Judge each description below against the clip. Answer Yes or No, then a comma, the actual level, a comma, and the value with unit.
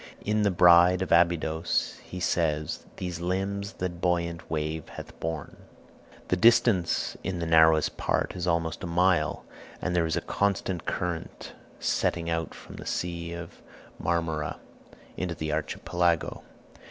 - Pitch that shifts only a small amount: Yes, narrow, 1.9 semitones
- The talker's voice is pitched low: Yes, very low, 85 Hz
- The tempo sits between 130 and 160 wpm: Yes, average, 140 wpm